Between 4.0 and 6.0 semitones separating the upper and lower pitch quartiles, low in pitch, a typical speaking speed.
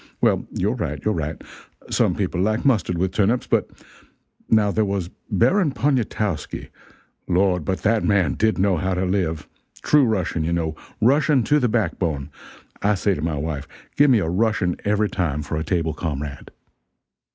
Yes: average, 5.1 semitones; very low, 95 Hz; average, 175 wpm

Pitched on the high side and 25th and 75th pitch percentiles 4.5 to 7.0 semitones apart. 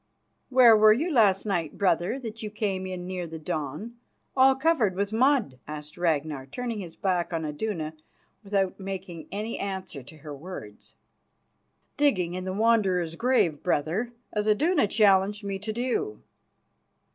Yes: high, 195 Hz; average, 4.9 semitones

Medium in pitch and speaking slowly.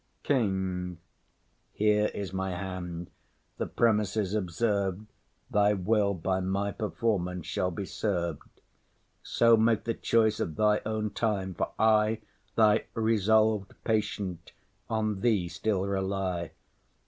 No: low, 100 Hz; slow, 115 wpm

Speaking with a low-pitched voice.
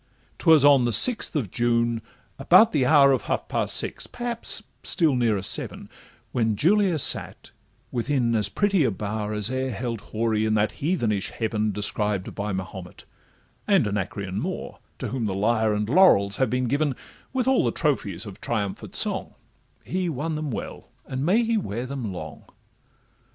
Yes: low, 120 Hz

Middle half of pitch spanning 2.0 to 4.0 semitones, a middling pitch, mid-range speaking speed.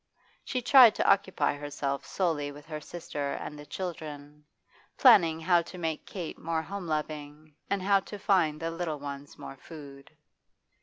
Yes: average, 3.6 semitones; medium, 160 Hz; average, 160 wpm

